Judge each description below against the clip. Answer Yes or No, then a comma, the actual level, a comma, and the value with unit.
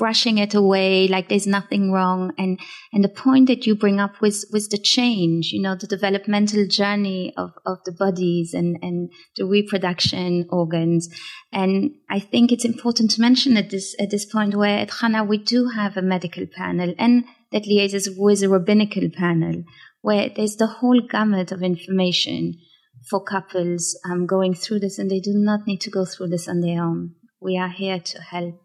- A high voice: Yes, high, 195 Hz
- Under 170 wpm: No, average, 190 wpm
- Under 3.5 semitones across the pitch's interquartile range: Yes, average, 2.8 semitones